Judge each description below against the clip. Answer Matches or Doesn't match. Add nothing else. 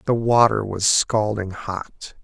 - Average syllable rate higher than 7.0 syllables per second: Doesn't match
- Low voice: Matches